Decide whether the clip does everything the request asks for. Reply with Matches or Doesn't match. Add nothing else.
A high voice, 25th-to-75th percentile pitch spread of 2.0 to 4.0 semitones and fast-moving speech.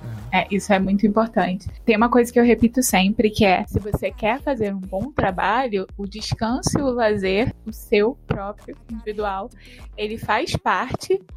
Doesn't match